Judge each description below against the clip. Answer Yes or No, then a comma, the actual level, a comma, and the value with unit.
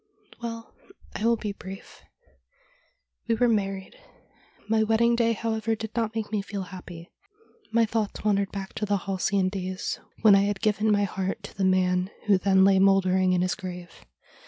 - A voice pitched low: No, high, 200 Hz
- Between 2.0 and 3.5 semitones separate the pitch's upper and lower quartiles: Yes, average, 2.7 semitones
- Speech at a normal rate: Yes, average, 180 wpm